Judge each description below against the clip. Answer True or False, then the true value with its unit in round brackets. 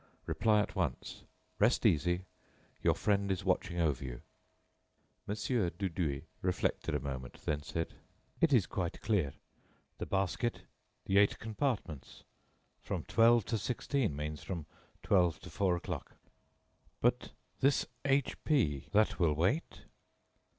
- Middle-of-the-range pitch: False (95 Hz)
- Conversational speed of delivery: False (130 wpm)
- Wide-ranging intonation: True (6.0 semitones)